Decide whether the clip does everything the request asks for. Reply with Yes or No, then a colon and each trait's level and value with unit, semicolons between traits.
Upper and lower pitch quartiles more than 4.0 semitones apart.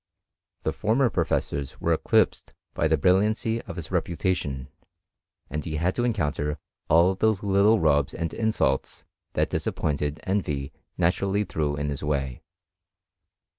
Yes: average, 5.1 semitones